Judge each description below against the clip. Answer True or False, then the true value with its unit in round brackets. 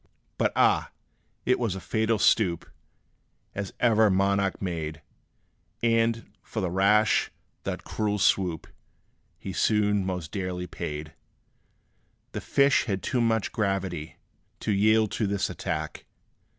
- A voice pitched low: True (100 Hz)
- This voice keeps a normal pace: False (125 wpm)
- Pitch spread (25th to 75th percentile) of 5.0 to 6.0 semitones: False (3.1 semitones)